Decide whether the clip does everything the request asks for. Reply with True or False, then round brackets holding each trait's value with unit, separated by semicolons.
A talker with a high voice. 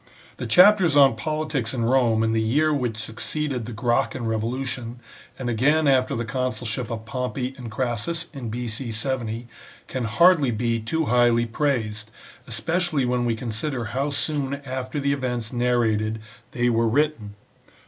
False (125 Hz)